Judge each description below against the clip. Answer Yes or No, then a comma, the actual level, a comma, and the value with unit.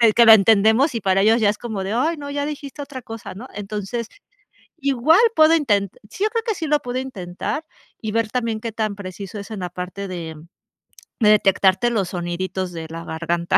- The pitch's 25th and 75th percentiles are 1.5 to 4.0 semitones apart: No, average, 5.3 semitones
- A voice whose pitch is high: Yes, high, 215 Hz